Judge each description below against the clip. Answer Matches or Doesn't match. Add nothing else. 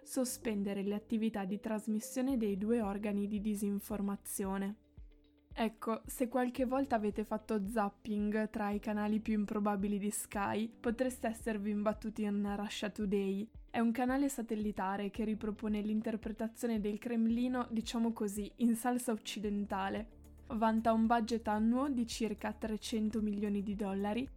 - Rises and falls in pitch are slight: Matches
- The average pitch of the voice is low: Doesn't match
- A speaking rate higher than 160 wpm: Doesn't match